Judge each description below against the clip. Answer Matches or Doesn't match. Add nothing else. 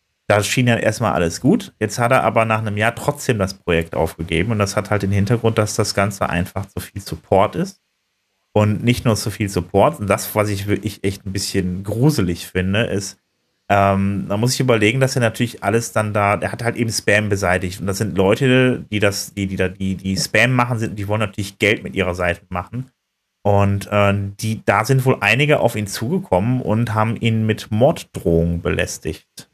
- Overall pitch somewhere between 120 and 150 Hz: Doesn't match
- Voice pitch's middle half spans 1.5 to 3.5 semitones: Matches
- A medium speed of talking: Doesn't match